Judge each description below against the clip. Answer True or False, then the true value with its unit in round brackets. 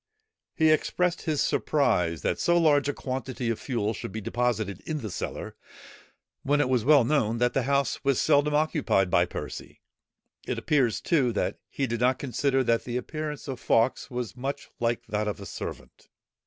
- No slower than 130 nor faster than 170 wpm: False (180 wpm)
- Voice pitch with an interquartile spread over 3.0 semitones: True (4.1 semitones)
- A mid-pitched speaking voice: False (130 Hz)